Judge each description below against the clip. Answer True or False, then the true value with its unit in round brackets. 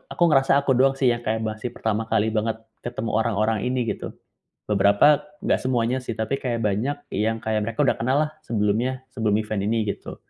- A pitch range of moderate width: True (3.0 semitones)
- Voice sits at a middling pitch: False (115 Hz)